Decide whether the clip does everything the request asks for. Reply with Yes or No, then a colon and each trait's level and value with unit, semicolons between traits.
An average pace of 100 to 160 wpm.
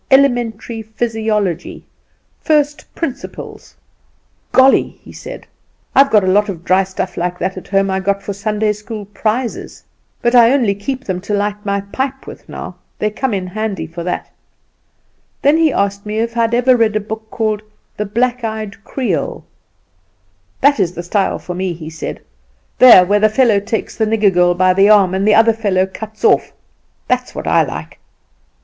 No: average, 180 wpm